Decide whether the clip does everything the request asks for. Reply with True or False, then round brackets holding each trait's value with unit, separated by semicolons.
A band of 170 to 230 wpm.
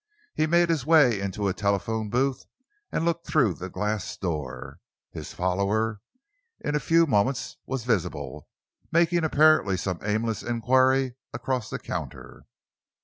False (140 wpm)